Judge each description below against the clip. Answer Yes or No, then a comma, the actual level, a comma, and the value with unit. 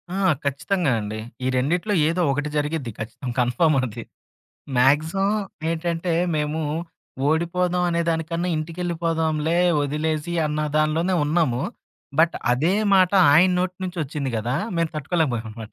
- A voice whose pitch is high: No, medium, 160 Hz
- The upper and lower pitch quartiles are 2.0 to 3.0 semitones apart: No, average, 3.4 semitones